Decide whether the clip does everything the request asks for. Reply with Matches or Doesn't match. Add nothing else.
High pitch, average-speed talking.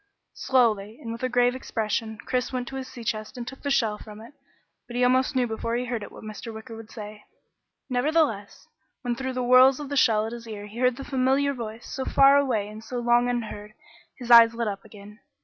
Doesn't match